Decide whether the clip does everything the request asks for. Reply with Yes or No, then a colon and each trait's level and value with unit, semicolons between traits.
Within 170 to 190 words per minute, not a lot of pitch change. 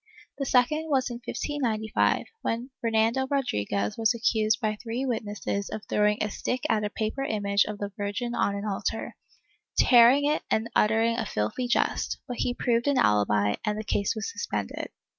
No: average, 175 wpm; average, 3.0 semitones